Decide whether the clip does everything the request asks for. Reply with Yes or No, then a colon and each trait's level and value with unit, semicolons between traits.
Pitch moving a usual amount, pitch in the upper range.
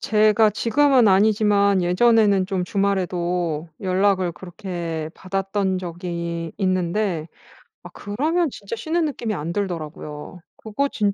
Yes: average, 3.5 semitones; high, 195 Hz